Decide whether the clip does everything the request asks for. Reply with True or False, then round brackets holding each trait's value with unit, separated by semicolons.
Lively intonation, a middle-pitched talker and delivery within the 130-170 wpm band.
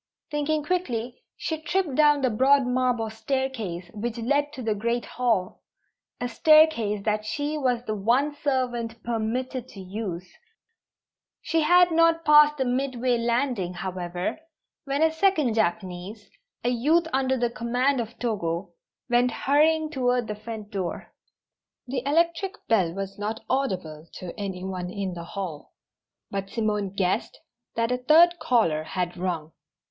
False (5.9 semitones; 240 Hz; 145 wpm)